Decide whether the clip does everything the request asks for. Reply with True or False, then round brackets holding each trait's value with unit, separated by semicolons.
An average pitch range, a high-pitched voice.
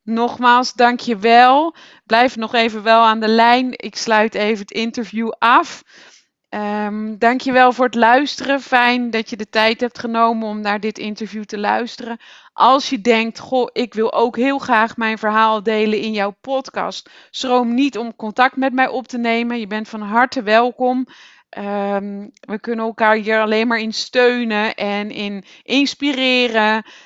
False (2.3 semitones; 230 Hz)